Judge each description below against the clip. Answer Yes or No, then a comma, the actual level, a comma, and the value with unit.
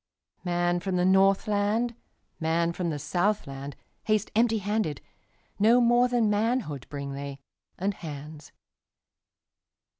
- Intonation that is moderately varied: No, wide, 6.0 semitones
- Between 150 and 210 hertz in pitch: Yes, high, 190 Hz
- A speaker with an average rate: No, slow, 90 wpm